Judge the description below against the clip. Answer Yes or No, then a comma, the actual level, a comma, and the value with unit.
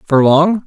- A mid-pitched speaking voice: Yes, medium, 160 Hz